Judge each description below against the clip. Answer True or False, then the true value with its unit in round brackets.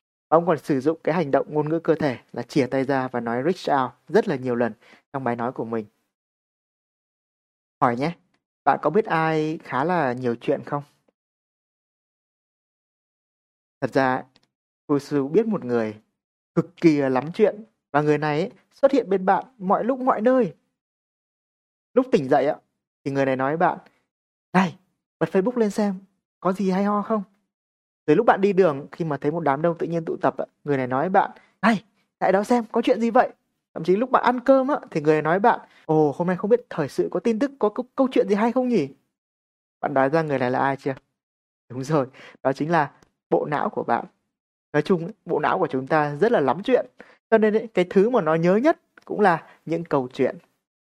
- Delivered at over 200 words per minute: True (210 wpm)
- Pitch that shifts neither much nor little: False (7.7 semitones)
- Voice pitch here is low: False (165 Hz)